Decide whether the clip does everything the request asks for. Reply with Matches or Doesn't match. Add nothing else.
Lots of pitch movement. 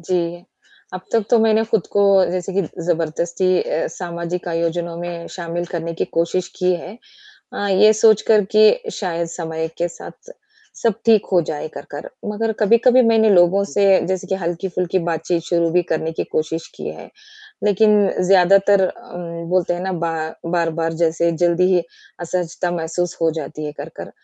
Doesn't match